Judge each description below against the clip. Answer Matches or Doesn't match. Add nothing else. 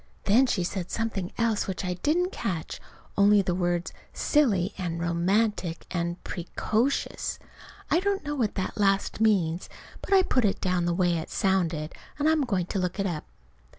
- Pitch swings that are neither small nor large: Matches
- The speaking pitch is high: Matches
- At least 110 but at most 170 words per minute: Doesn't match